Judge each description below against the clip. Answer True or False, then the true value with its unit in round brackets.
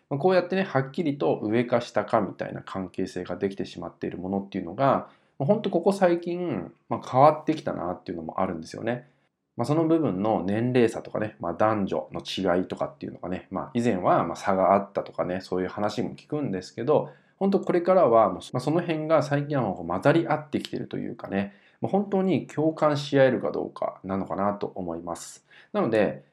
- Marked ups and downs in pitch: True (8.5 semitones)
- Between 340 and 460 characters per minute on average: True (385 characters per minute)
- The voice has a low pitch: True (120 Hz)